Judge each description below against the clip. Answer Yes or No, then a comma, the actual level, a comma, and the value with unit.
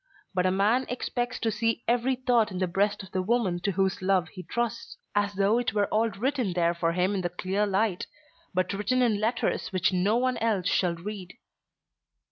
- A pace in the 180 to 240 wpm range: Yes, fast, 205 wpm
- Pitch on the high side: Yes, high, 205 Hz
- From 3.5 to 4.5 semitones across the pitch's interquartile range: Yes, average, 3.8 semitones